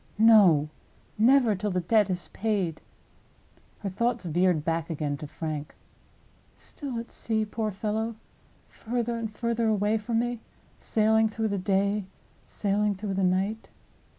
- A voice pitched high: Yes, high, 210 Hz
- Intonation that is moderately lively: Yes, average, 3.3 semitones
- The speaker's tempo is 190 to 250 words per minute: No, average, 140 wpm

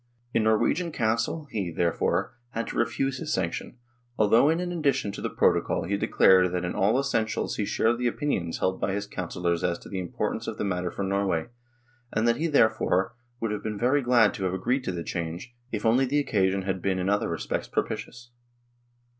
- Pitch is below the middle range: Yes, low, 105 Hz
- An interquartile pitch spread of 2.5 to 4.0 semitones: No, average, 4.7 semitones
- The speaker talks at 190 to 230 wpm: Yes, fast, 205 wpm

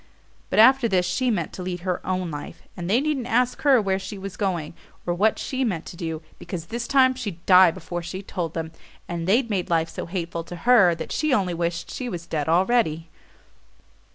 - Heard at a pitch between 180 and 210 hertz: Yes, medium, 185 Hz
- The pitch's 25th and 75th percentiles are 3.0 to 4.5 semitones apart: No, wide, 5.4 semitones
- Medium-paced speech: No, fast, 210 wpm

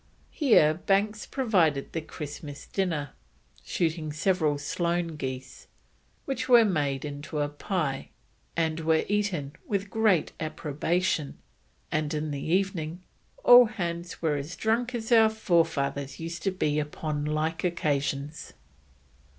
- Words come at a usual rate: No, slow, 125 wpm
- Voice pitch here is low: No, medium, 160 Hz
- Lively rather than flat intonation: No, average, 4.7 semitones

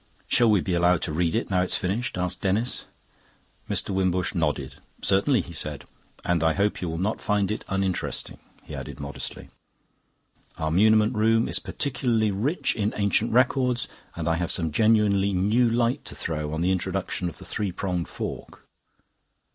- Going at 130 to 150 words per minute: No, average, 170 wpm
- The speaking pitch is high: No, very low, 95 Hz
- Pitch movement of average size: Yes, average, 4.2 semitones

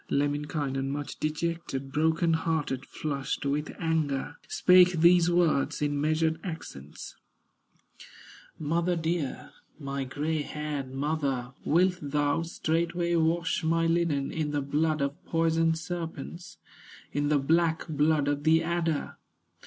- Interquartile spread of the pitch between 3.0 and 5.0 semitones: No, narrow, 2.5 semitones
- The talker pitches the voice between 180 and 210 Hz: No, medium, 155 Hz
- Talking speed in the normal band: No, slow, 120 wpm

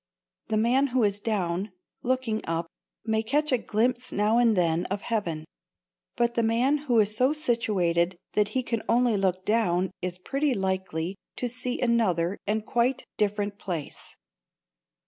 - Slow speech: No, average, 155 wpm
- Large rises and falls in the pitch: No, average, 4.4 semitones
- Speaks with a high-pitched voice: Yes, high, 215 Hz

